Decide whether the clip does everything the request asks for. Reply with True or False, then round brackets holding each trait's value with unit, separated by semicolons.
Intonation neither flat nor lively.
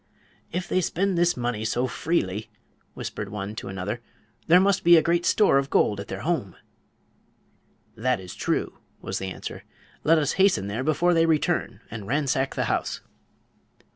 False (8.5 semitones)